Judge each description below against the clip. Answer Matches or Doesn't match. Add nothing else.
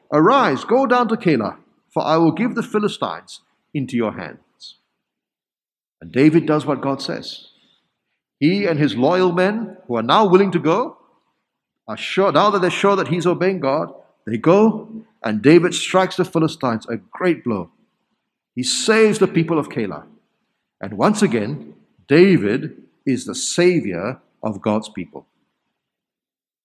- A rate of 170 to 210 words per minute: Doesn't match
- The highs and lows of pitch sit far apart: Matches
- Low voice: Doesn't match